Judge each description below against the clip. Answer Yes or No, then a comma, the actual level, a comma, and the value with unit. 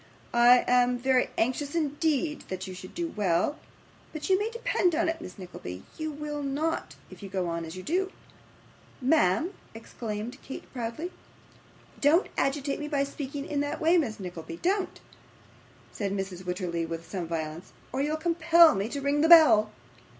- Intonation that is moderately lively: No, wide, 8.4 semitones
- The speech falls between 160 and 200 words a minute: Yes, average, 170 wpm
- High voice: Yes, very high, 270 Hz